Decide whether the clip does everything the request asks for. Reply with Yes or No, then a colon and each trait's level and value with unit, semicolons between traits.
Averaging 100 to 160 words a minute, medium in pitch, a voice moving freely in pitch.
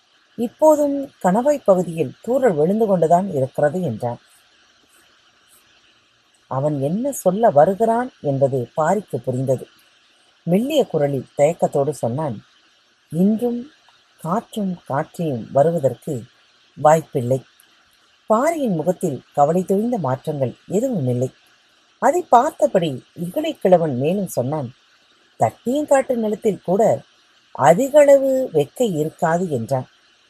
No: average, 85 wpm; medium, 175 Hz; wide, 8.5 semitones